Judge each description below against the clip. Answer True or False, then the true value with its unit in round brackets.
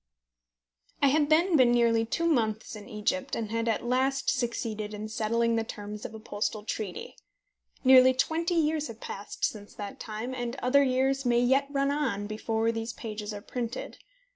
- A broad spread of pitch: False (3.8 semitones)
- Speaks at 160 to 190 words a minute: True (175 wpm)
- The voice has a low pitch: False (235 Hz)